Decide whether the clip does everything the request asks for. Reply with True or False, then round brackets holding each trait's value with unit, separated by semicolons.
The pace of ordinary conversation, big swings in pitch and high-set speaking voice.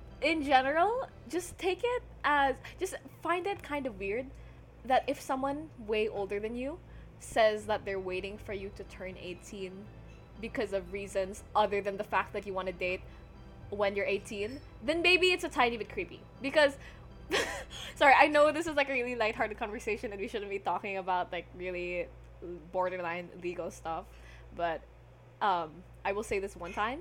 True (180 wpm; 6.9 semitones; 210 Hz)